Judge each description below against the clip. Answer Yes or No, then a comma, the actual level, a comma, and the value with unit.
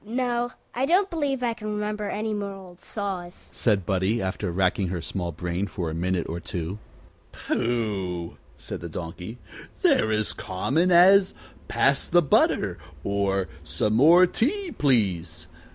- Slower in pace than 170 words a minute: Yes, average, 150 wpm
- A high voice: No, low, 115 Hz